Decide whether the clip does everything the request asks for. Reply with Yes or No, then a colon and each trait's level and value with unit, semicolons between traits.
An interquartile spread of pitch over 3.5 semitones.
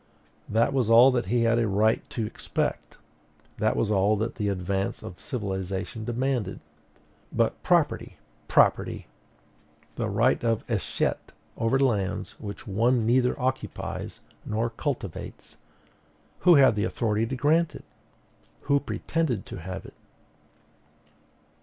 Yes: average, 3.9 semitones